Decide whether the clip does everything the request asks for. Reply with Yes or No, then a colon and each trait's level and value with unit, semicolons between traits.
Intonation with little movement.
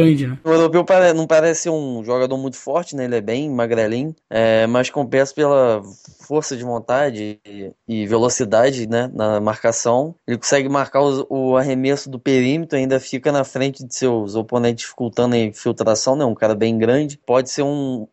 No: average, 3.4 semitones